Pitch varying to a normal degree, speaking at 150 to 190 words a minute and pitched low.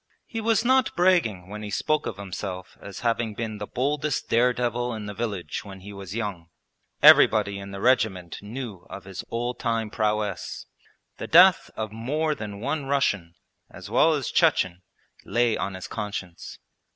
Yes: average, 4.1 semitones; average, 170 wpm; low, 110 Hz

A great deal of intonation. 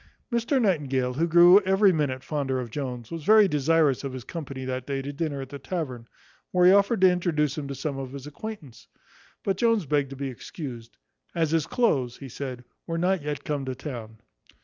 No: average, 4.8 semitones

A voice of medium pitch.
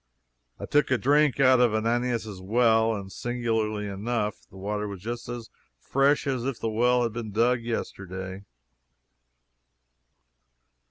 No: low, 115 Hz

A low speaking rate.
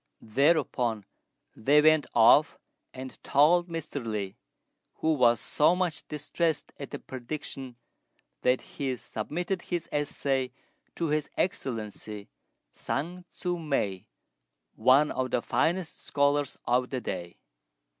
Yes: slow, 115 wpm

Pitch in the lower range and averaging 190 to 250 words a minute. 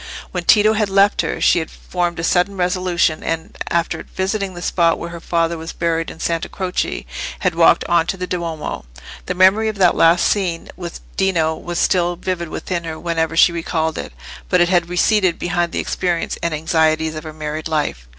No: medium, 170 Hz; average, 200 wpm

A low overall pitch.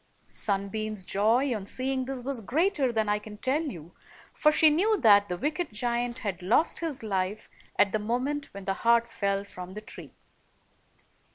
No: high, 230 Hz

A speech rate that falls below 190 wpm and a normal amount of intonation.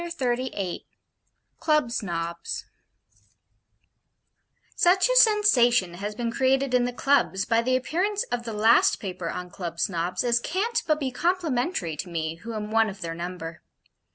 No: average, 155 wpm; wide, 7.5 semitones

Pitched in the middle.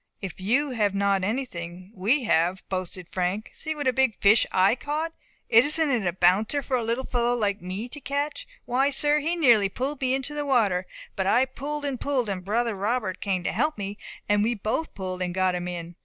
No: high, 220 Hz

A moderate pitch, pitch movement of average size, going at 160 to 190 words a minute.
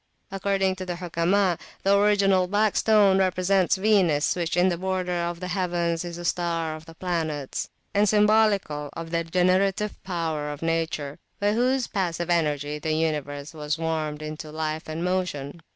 Yes: medium, 175 Hz; average, 3.3 semitones; average, 170 wpm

